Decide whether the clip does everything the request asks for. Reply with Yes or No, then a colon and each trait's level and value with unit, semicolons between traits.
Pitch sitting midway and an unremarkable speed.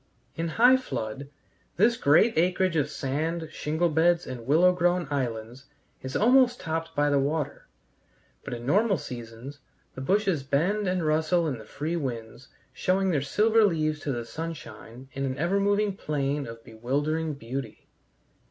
Yes: medium, 155 Hz; average, 155 wpm